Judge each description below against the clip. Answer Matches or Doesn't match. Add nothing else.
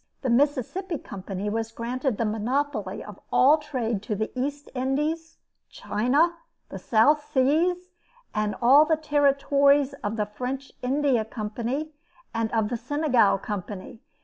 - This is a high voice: Matches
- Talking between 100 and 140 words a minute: Matches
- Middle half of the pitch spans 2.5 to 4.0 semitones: Doesn't match